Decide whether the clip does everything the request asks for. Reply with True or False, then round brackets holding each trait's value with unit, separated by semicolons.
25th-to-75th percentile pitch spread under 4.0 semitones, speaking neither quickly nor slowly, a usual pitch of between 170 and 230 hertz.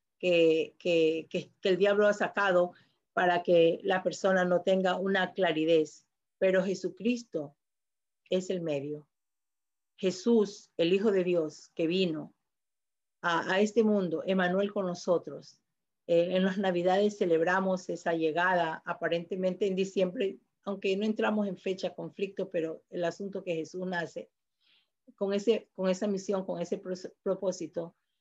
True (2.5 semitones; 140 wpm; 185 Hz)